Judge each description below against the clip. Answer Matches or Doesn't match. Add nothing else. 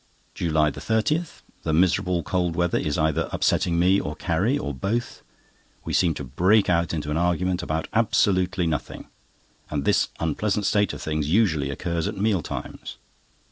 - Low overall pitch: Matches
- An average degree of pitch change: Matches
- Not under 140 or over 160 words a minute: Matches